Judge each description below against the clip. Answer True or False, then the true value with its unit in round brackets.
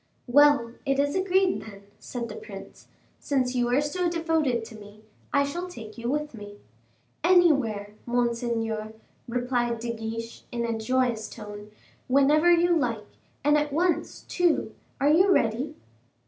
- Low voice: False (250 Hz)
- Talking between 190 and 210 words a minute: False (145 wpm)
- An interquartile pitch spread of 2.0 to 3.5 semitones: False (4.8 semitones)